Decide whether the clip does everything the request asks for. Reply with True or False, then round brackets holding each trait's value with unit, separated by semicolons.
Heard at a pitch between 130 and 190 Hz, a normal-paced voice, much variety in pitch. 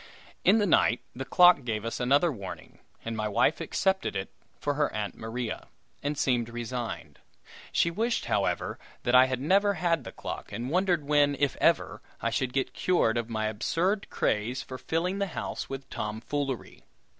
True (135 Hz; 175 wpm; 6.5 semitones)